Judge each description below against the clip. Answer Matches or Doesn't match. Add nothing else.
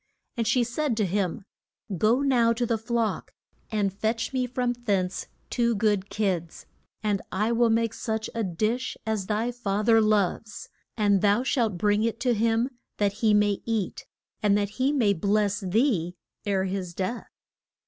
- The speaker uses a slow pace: Doesn't match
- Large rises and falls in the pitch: Doesn't match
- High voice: Matches